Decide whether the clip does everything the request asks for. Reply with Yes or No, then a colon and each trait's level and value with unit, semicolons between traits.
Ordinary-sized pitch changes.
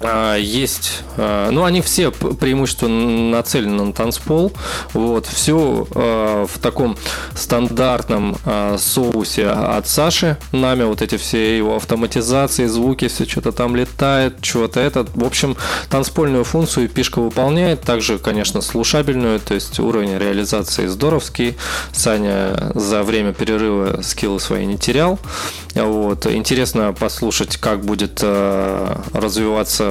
Yes: average, 3.6 semitones